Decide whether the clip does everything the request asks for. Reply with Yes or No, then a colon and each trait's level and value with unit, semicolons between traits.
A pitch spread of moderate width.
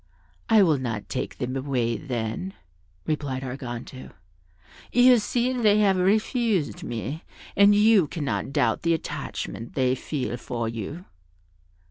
No: wide, 8.5 semitones